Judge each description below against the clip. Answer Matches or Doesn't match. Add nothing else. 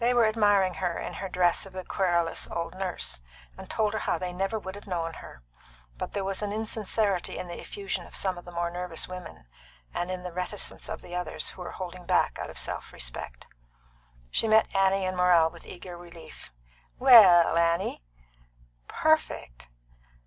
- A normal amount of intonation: Doesn't match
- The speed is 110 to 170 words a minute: Doesn't match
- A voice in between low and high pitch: Matches